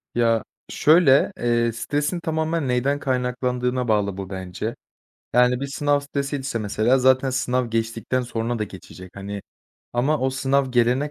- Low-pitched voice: Yes, low, 125 Hz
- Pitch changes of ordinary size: Yes, average, 3.2 semitones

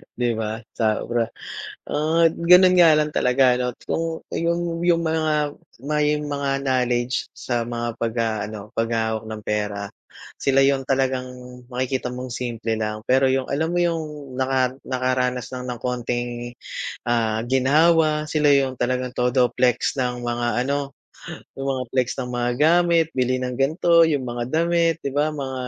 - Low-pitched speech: Yes, low, 130 Hz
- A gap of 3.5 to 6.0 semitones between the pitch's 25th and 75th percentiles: Yes, average, 3.8 semitones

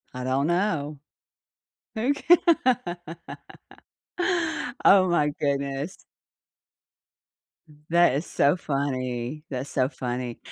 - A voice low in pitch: No, medium, 145 Hz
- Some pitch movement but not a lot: Yes, average, 5.0 semitones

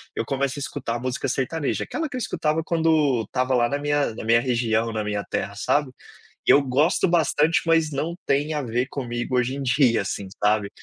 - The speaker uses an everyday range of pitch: Yes, average, 4.2 semitones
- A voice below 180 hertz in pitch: Yes, low, 135 Hz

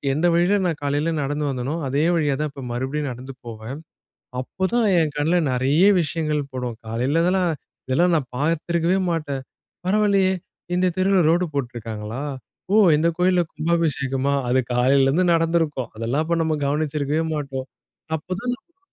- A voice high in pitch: No, medium, 150 Hz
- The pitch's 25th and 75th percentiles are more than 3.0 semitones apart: Yes, average, 4.3 semitones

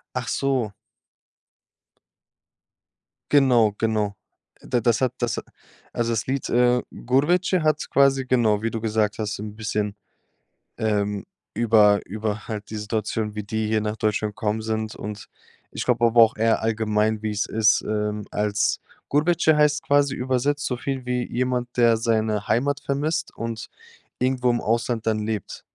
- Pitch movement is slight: No, average, 3.0 semitones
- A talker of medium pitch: No, low, 115 Hz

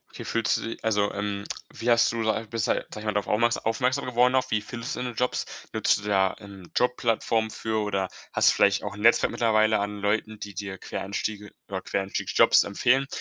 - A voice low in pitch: Yes, low, 110 Hz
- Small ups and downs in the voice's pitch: Yes, narrow, 2.3 semitones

